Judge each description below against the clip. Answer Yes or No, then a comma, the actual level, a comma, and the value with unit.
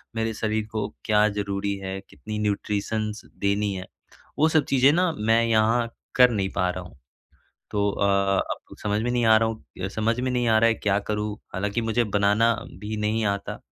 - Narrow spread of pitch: Yes, narrow, 2.0 semitones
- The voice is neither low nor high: No, low, 105 Hz